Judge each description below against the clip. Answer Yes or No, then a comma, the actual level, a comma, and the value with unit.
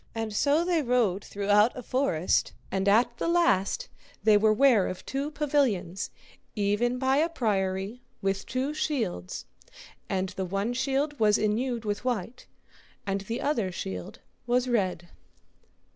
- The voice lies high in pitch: Yes, high, 225 Hz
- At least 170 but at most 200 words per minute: No, average, 145 wpm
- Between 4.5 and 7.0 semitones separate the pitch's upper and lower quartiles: Yes, average, 5.2 semitones